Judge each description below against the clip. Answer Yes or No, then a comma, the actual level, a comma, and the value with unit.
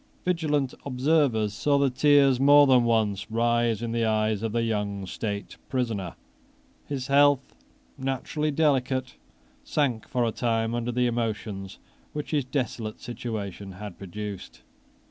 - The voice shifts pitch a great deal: No, average, 4.1 semitones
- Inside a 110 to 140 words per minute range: Yes, slow, 135 wpm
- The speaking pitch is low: Yes, low, 120 Hz